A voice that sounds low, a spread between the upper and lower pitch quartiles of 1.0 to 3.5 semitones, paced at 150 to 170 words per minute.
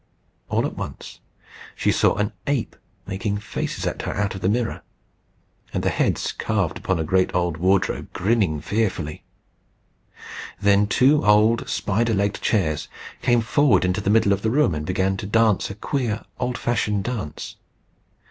Yes: low, 100 Hz; average, 3.2 semitones; average, 160 wpm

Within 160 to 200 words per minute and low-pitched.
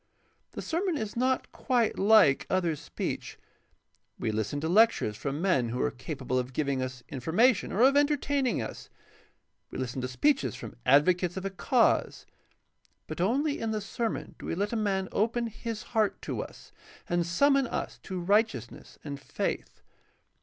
No: average, 165 wpm; high, 190 Hz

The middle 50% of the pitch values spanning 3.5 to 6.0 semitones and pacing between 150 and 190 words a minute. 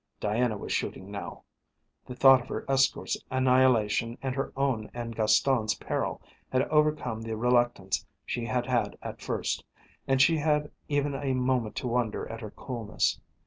No: average, 2.9 semitones; average, 160 wpm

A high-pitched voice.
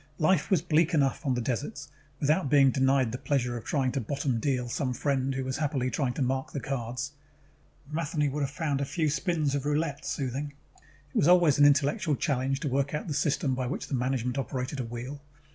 No: medium, 140 Hz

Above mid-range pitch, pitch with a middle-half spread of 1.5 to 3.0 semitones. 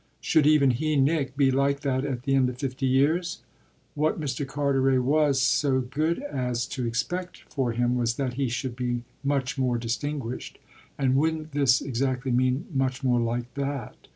No: low, 135 Hz; narrow, 2.4 semitones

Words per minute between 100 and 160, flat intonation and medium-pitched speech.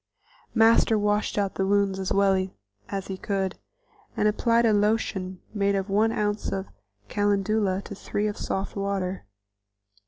No: average, 145 wpm; narrow, 1.5 semitones; high, 200 Hz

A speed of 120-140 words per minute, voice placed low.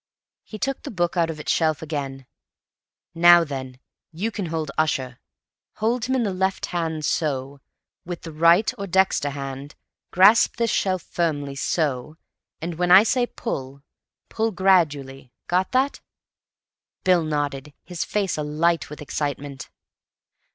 No: slow, 135 wpm; medium, 165 Hz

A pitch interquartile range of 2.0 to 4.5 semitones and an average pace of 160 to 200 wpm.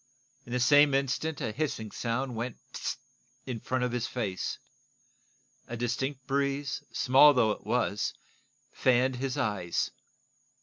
No: narrow, 2.6 semitones; slow, 135 wpm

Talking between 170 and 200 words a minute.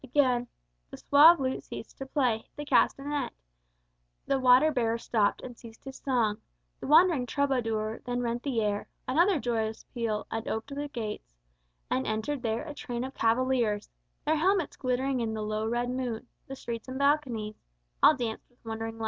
Yes: average, 175 wpm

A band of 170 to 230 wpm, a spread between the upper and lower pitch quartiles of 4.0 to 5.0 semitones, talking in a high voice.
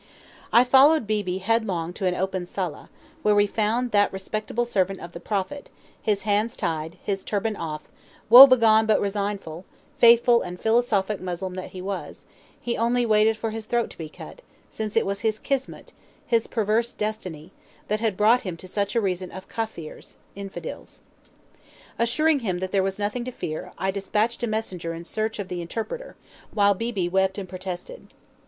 No: average, 175 wpm; average, 3.4 semitones; high, 205 Hz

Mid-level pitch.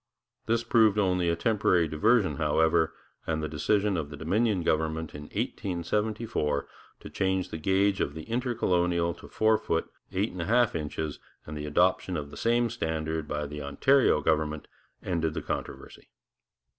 No: very low, 85 Hz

